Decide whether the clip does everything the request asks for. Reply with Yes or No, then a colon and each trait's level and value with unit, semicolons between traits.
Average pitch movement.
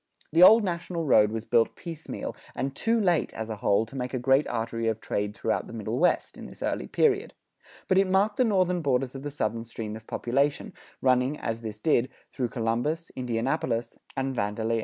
No: wide, 6.5 semitones